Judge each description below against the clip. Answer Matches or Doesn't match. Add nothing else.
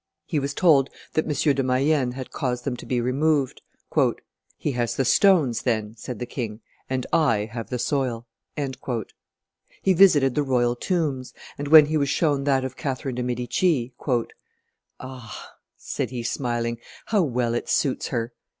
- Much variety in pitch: Doesn't match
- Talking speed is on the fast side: Doesn't match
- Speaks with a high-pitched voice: Doesn't match